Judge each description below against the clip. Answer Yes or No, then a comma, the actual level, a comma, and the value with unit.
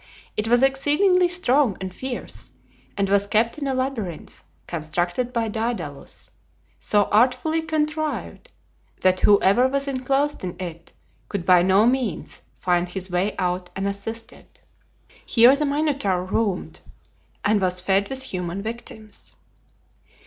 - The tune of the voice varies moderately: No, wide, 6.2 semitones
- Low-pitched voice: No, high, 220 Hz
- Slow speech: Yes, slow, 125 wpm